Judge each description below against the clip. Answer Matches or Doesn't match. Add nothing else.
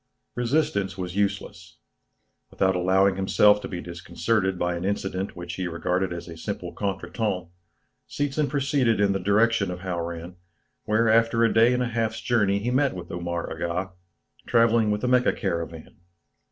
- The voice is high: Doesn't match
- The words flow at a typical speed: Matches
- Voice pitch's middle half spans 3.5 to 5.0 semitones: Matches